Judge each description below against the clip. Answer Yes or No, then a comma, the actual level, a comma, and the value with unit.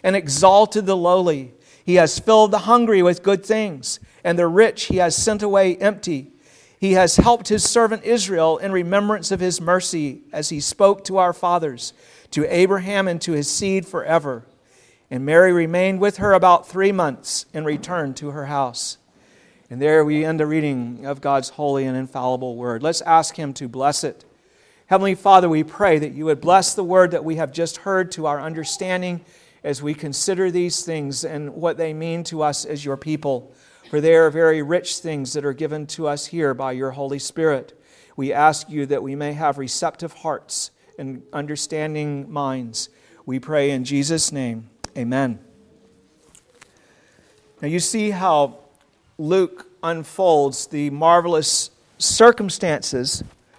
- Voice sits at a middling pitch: Yes, medium, 160 Hz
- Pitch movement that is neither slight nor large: Yes, average, 4.3 semitones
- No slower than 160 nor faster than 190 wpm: Yes, average, 170 wpm